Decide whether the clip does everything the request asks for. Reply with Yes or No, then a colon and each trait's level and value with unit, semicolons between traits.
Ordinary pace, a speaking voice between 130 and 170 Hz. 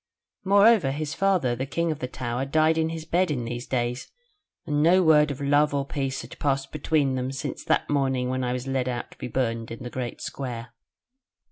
No: fast, 215 wpm; low, 135 Hz